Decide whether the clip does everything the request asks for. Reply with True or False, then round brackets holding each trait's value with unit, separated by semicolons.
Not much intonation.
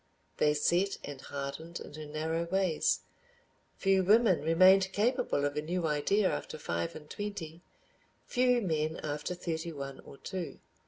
False (4.1 semitones)